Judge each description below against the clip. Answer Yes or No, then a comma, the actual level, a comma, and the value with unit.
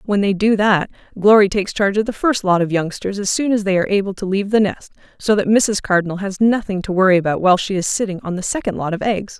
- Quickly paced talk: Yes, fast, 270 wpm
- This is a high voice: Yes, high, 200 Hz